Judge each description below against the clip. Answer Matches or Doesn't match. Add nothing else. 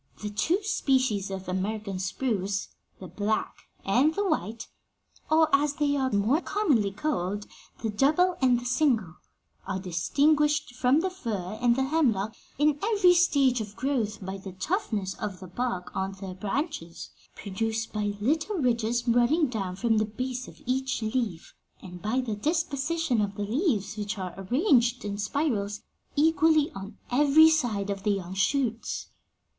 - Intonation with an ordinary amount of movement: Doesn't match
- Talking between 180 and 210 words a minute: Doesn't match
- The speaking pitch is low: Doesn't match